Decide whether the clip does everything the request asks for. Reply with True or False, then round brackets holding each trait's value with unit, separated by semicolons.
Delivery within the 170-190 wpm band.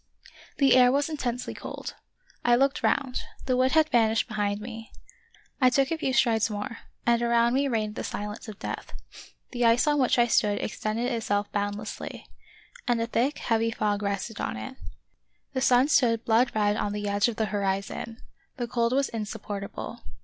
True (185 wpm)